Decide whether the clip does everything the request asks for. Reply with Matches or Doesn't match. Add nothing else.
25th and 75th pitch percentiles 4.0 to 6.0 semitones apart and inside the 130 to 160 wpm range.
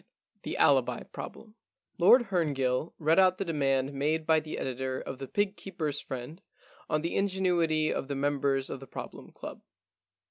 Doesn't match